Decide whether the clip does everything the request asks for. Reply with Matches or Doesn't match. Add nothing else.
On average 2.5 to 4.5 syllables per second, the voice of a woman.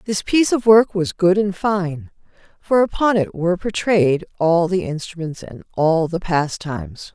Matches